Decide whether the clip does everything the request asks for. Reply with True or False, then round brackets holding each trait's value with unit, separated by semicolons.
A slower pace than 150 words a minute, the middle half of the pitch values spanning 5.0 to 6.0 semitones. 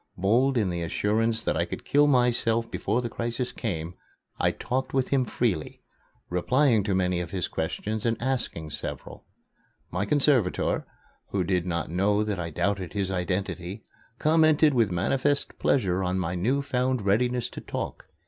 False (160 wpm; 5.5 semitones)